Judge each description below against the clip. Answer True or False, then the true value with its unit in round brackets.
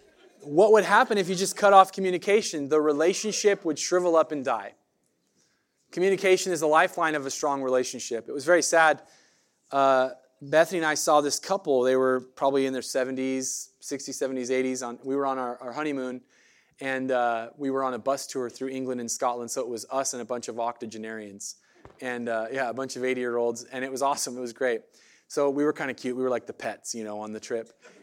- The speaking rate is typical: False (225 wpm)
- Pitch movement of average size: True (3.5 semitones)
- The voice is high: False (135 Hz)